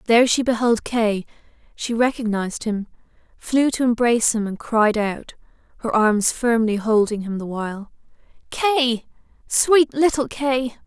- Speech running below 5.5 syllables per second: Yes, 4.6 syllables/s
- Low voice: No, high, 235 Hz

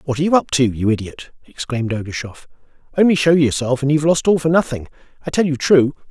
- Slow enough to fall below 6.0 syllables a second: No, 6.6 syllables/s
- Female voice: No, male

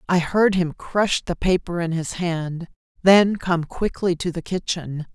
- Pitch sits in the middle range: Yes, medium, 175 Hz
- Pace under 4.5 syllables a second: Yes, 4.0 syllables/s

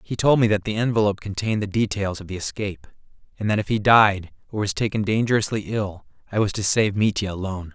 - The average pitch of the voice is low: Yes, low, 100 Hz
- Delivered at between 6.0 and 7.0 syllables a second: Yes, 6.3 syllables/s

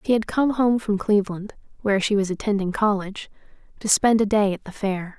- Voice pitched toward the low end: No, high, 205 Hz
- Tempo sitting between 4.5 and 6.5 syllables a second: Yes, 5.8 syllables/s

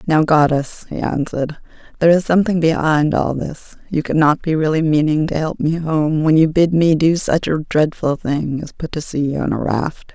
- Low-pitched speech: No, medium, 155 Hz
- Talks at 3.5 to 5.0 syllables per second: Yes, 4.9 syllables/s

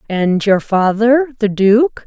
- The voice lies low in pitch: No, high, 220 Hz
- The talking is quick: No, slow, 115 wpm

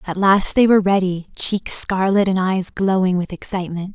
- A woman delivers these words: Yes, female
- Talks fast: No, average, 180 wpm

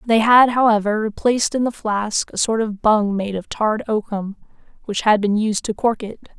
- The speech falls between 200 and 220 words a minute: Yes, fast, 205 wpm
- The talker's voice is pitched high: Yes, high, 215 Hz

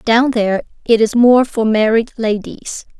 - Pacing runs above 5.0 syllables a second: No, 4.3 syllables/s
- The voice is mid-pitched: No, high, 225 Hz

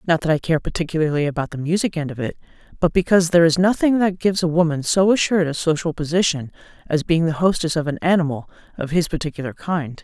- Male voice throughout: No, female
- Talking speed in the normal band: No, fast, 215 wpm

